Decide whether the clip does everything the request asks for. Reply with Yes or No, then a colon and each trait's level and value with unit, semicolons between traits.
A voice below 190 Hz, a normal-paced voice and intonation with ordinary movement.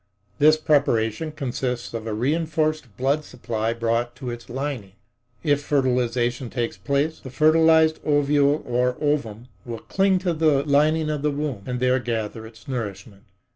Yes: low, 135 Hz; average, 150 wpm; average, 4.3 semitones